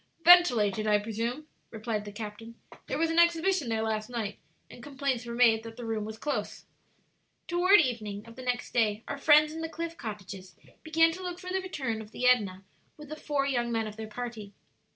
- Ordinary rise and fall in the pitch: No, wide, 6.0 semitones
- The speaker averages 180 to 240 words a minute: Yes, fast, 205 wpm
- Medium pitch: No, high, 235 Hz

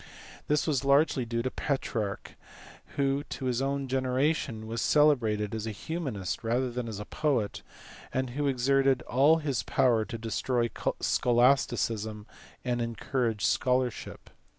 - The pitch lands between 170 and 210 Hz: No, low, 125 Hz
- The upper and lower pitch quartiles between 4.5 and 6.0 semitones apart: No, average, 3.2 semitones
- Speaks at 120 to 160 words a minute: Yes, average, 140 wpm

